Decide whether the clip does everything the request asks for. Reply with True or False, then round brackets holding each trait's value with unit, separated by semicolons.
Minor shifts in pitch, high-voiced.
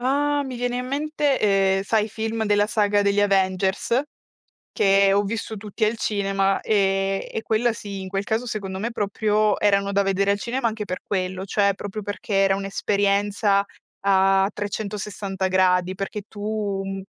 True (1.9 semitones; 200 Hz)